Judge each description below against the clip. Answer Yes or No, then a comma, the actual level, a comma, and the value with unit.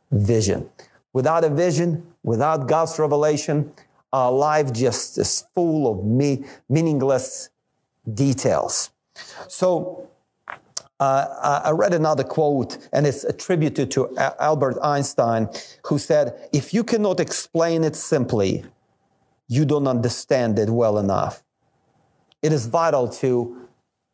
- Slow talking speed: Yes, slow, 115 wpm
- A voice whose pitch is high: No, medium, 145 Hz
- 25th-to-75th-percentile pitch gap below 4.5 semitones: Yes, average, 3.8 semitones